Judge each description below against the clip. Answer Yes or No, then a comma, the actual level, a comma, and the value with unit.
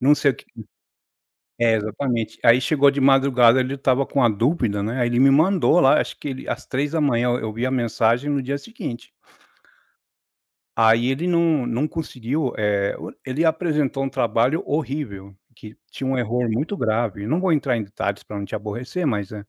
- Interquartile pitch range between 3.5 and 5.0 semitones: Yes, average, 4.0 semitones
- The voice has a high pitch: No, low, 130 Hz